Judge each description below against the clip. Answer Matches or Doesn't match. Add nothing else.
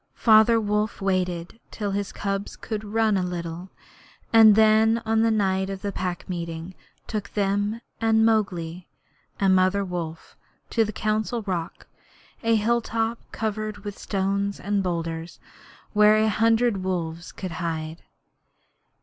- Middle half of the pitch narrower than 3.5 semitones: Matches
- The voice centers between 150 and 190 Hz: Doesn't match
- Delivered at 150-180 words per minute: Doesn't match